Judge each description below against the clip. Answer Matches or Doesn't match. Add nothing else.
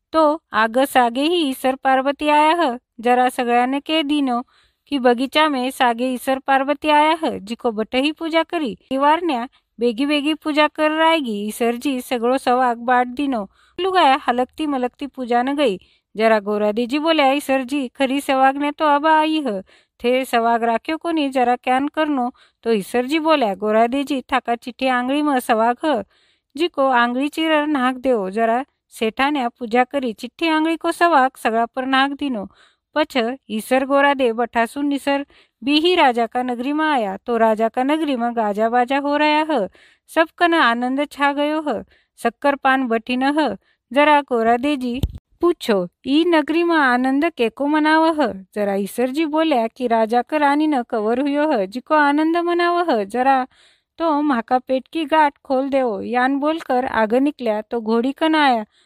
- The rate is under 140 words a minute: Doesn't match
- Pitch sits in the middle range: Doesn't match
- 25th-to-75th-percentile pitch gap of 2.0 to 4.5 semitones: Matches